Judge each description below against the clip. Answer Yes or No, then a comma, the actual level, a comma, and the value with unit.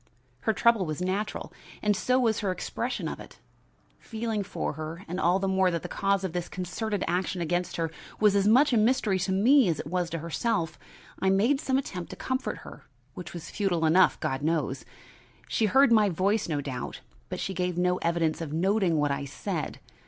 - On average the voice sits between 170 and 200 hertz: Yes, medium, 185 Hz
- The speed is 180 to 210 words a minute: Yes, fast, 205 wpm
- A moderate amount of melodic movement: Yes, average, 4.1 semitones